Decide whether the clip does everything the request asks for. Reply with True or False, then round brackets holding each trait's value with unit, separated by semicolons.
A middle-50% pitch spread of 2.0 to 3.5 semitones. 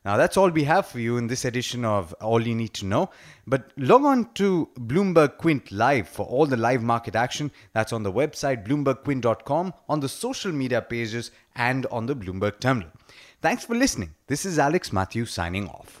False (4.7 semitones)